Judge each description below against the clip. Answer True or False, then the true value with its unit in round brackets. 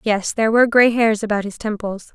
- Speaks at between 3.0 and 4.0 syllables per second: False (5.9 syllables/s)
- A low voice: False (215 Hz)